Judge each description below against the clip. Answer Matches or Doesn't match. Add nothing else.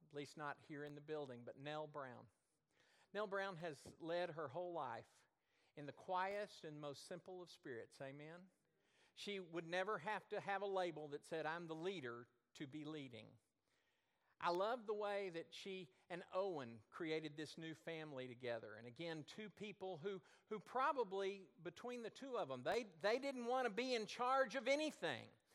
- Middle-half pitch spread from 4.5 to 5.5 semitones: Matches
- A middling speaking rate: Matches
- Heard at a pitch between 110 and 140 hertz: Doesn't match